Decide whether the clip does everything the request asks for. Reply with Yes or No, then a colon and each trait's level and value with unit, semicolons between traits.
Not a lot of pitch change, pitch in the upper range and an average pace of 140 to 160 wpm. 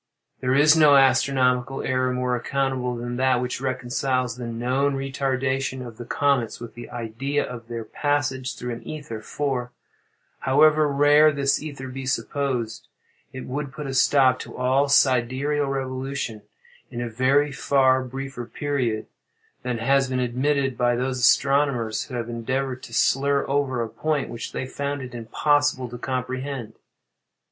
No: narrow, 2.2 semitones; low, 130 Hz; average, 155 wpm